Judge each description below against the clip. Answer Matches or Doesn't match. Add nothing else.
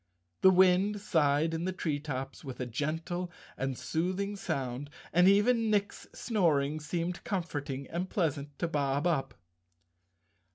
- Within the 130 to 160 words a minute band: Matches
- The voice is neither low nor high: Matches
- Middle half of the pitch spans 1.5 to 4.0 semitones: Doesn't match